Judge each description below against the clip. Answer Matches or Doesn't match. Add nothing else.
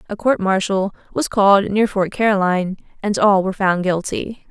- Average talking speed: Matches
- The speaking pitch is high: Matches